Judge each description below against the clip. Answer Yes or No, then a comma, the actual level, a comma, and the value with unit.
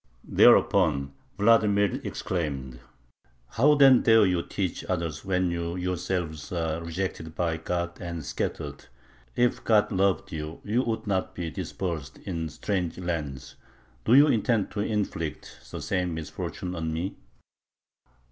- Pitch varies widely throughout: No, average, 4.0 semitones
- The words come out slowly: Yes, slow, 130 wpm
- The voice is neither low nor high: No, very low, 90 Hz